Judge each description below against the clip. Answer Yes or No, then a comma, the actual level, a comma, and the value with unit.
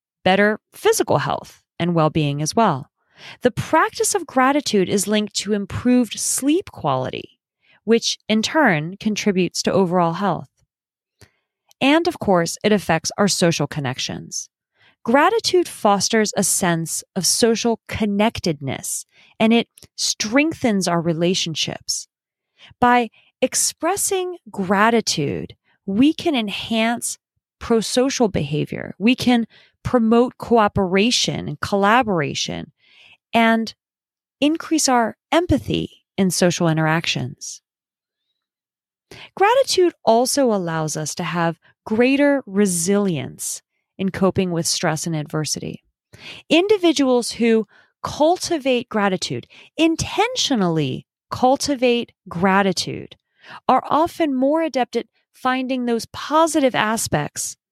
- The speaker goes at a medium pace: No, slow, 100 wpm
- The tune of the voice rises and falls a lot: Yes, wide, 6.1 semitones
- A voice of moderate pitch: No, high, 220 Hz